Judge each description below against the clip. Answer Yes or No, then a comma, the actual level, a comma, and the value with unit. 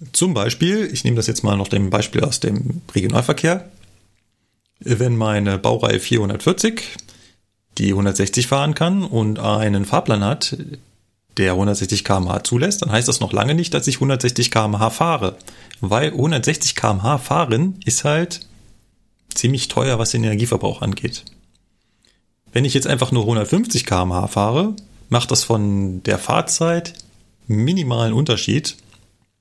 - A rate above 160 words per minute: No, average, 135 wpm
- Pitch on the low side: Yes, low, 115 Hz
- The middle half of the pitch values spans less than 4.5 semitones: No, average, 5.2 semitones